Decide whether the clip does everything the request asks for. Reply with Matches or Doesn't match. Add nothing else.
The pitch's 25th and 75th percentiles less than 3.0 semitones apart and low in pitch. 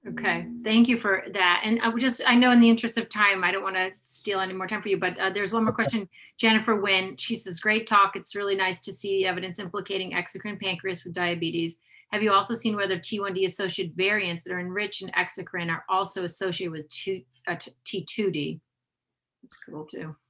Doesn't match